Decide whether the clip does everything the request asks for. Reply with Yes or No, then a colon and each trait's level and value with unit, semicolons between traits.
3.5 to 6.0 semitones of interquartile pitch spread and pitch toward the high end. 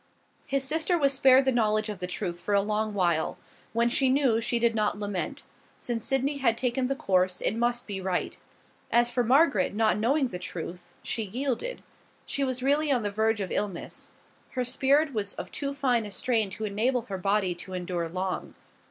Yes: average, 4.9 semitones; high, 230 Hz